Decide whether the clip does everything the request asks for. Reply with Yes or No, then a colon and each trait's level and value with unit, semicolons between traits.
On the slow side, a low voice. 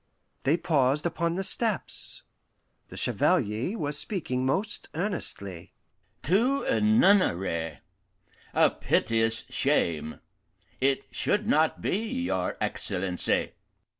No: slow, 100 wpm; medium, 145 Hz